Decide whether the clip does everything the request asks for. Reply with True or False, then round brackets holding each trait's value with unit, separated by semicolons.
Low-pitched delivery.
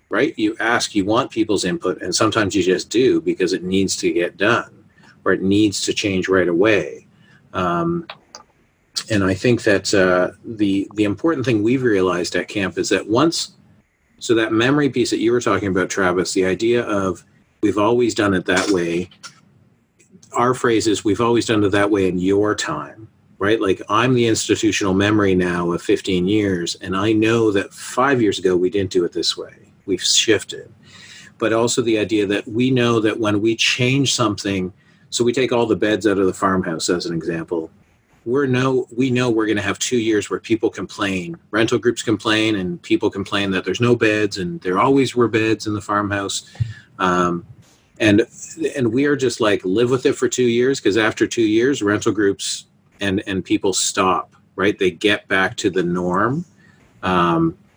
True (110 Hz)